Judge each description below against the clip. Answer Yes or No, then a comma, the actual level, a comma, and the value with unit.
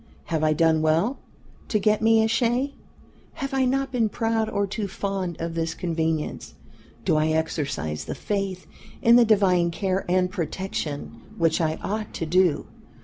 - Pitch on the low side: No, medium, 185 Hz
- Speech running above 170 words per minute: No, average, 165 wpm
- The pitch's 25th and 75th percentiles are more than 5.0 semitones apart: Yes, wide, 5.4 semitones